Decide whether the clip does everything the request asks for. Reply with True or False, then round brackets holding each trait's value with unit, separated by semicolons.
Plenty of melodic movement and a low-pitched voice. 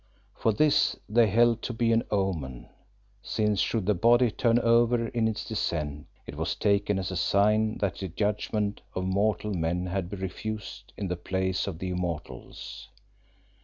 False (3.2 semitones; 100 Hz)